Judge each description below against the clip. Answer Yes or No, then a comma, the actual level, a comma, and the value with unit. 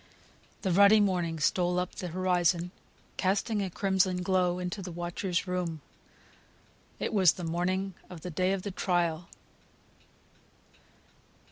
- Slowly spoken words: Yes, slow, 125 wpm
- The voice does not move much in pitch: Yes, narrow, 1.5 semitones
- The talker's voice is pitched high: No, medium, 180 Hz